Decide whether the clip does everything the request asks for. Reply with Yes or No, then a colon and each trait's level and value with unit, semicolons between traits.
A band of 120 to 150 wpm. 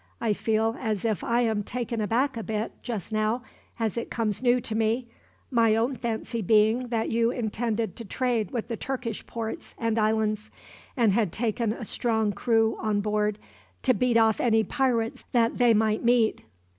No: average, 180 wpm